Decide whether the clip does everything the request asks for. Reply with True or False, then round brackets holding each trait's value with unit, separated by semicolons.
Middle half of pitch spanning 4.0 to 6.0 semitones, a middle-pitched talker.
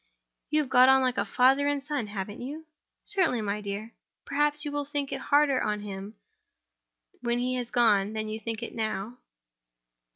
False (4.8 semitones; 245 Hz)